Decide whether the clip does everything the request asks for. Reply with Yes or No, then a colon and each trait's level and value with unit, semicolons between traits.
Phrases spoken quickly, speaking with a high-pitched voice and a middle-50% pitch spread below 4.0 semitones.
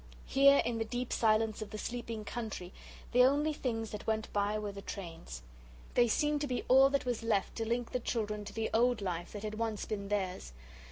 Yes: fast, 215 wpm; high, 225 Hz; average, 2.9 semitones